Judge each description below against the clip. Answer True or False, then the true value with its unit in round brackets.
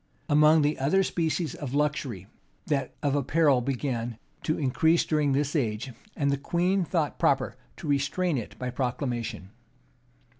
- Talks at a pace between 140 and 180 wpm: True (155 wpm)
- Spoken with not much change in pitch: False (3.4 semitones)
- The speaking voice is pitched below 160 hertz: True (140 Hz)